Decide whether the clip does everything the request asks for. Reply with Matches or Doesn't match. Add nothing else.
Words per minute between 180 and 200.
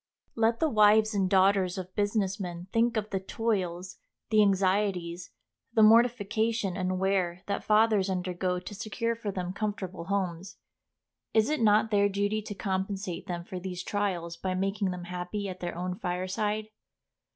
Doesn't match